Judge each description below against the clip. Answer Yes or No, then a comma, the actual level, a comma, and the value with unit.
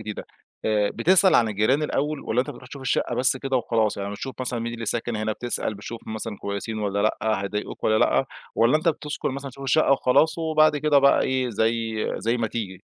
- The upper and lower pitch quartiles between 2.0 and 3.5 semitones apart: No, average, 4.2 semitones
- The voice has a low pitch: Yes, low, 120 Hz